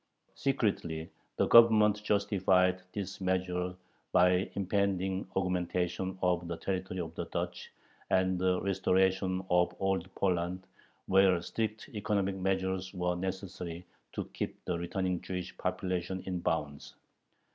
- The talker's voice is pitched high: No, very low, 95 Hz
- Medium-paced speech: No, slow, 125 wpm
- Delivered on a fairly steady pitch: Yes, narrow, 1.3 semitones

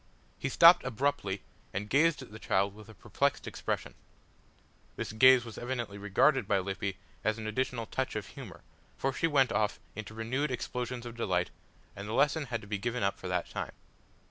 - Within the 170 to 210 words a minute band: Yes, average, 190 wpm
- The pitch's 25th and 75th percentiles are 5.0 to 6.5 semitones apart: No, average, 4.1 semitones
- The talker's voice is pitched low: Yes, low, 115 Hz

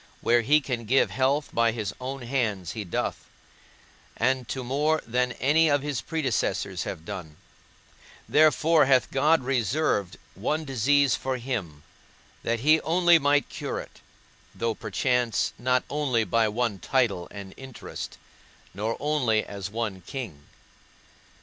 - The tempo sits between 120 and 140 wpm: Yes, slow, 135 wpm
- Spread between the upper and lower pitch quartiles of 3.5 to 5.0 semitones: Yes, average, 4.6 semitones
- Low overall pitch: Yes, low, 125 Hz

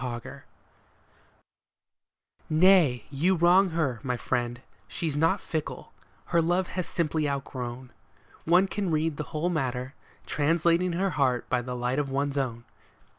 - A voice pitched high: No, medium, 150 Hz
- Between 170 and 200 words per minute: No, average, 140 wpm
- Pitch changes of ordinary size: Yes, average, 5.0 semitones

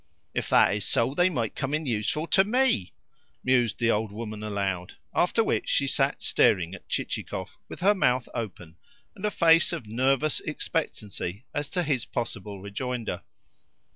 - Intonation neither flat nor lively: No, wide, 6.8 semitones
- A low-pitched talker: Yes, low, 120 Hz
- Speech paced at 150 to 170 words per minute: Yes, average, 165 wpm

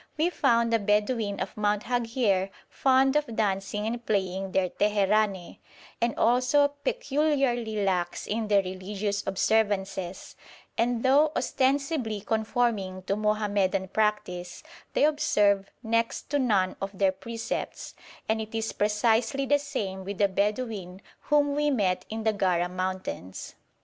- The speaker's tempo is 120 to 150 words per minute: Yes, slow, 135 wpm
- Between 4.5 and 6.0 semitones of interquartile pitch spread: No, average, 3.8 semitones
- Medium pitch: No, high, 215 Hz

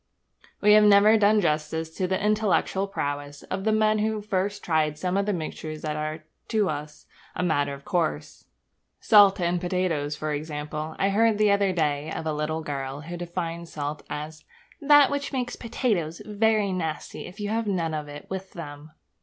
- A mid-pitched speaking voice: Yes, medium, 175 Hz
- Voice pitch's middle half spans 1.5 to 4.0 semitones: No, average, 5.2 semitones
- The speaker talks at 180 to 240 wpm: Yes, average, 185 wpm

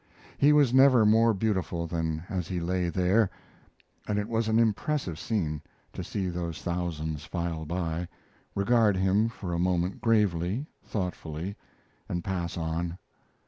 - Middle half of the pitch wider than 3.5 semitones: Yes, average, 4.2 semitones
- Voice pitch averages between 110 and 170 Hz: No, very low, 90 Hz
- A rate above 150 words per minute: No, average, 140 wpm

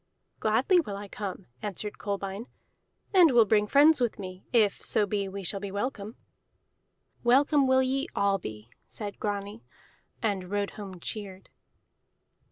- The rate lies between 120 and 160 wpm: Yes, average, 145 wpm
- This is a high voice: Yes, high, 205 Hz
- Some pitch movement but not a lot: Yes, average, 3.5 semitones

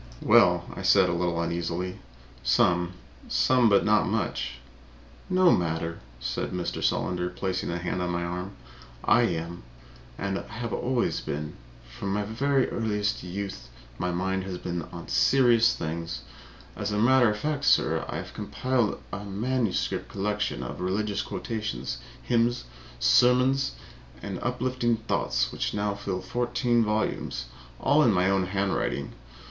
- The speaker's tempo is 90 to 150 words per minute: Yes, average, 140 wpm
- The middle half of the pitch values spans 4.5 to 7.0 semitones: Yes, average, 5.2 semitones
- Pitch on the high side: No, low, 100 Hz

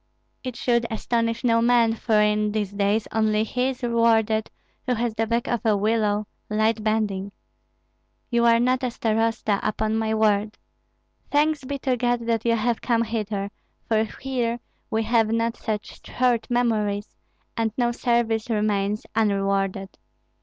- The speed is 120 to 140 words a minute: No, average, 155 wpm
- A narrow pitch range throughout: Yes, narrow, 1.9 semitones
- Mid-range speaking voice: No, high, 225 Hz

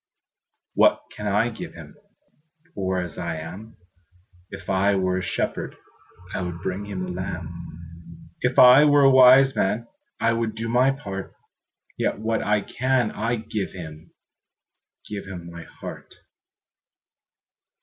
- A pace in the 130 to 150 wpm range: Yes, slow, 135 wpm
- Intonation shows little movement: No, average, 4.5 semitones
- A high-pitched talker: No, low, 100 Hz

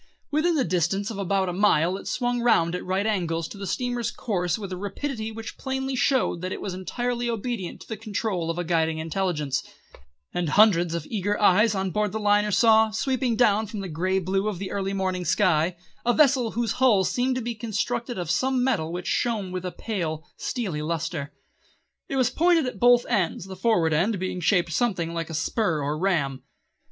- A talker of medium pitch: No, high, 195 Hz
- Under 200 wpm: No, fast, 205 wpm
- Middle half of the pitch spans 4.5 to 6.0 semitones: Yes, average, 5.0 semitones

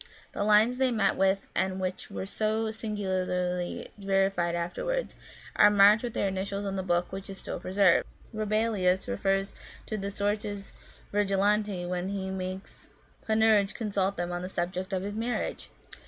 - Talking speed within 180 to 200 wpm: No, average, 155 wpm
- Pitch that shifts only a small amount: Yes, narrow, 2.0 semitones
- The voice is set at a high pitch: Yes, high, 195 Hz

